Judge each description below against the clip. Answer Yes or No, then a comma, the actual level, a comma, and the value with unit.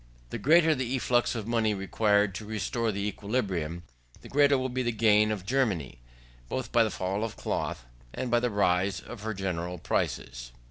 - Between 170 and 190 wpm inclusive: Yes, average, 185 wpm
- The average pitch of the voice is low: Yes, low, 105 Hz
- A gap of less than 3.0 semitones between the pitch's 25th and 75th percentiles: No, average, 4.0 semitones